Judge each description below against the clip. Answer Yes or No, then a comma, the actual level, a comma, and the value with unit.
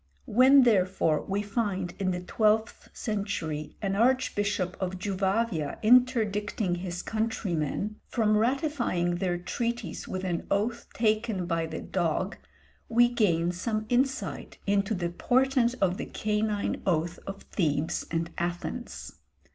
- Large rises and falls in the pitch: No, average, 4.5 semitones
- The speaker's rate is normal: No, slow, 130 wpm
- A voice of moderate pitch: No, high, 200 Hz